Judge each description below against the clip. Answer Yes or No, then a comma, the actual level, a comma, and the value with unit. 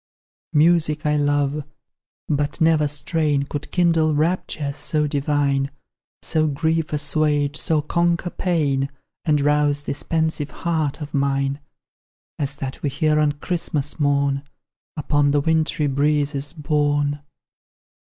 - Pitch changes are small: Yes, narrow, 1.6 semitones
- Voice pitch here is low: No, medium, 150 Hz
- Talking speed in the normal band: No, slow, 120 wpm